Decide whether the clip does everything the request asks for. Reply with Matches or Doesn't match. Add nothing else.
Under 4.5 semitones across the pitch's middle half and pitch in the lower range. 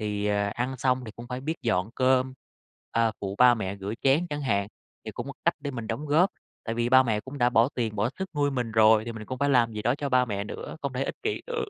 Matches